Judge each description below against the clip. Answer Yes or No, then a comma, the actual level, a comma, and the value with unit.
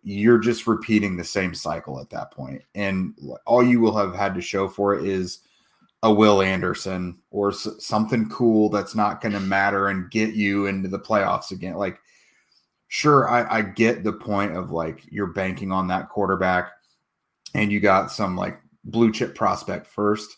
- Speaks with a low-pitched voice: Yes, low, 100 Hz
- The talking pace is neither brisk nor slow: Yes, average, 185 wpm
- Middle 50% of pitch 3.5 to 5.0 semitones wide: No, narrow, 2.5 semitones